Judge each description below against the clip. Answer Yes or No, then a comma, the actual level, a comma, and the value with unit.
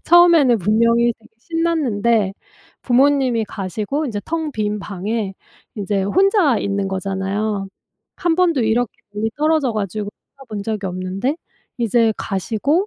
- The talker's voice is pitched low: No, high, 225 Hz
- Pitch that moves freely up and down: Yes, wide, 5.8 semitones